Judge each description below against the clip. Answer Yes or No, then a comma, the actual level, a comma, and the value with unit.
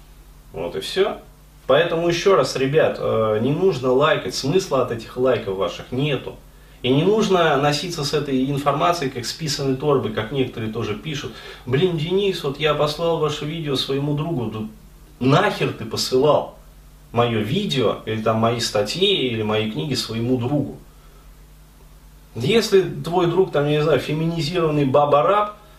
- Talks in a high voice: No, medium, 140 Hz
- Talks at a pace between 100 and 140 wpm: No, average, 150 wpm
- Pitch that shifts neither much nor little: No, wide, 5.9 semitones